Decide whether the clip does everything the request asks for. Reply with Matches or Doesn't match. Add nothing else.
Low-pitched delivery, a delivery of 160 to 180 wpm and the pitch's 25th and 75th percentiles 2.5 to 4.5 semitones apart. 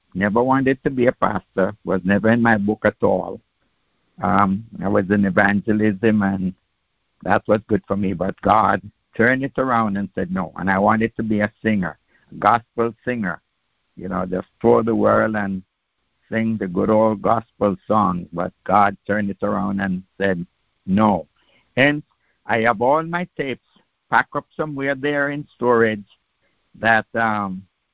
Matches